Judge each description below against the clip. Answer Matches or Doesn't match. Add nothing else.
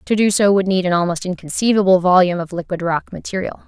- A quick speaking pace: Matches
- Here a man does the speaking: Doesn't match